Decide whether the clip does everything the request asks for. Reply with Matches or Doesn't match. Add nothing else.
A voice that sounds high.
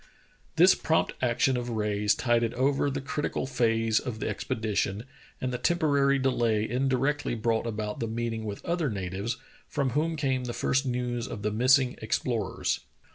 Doesn't match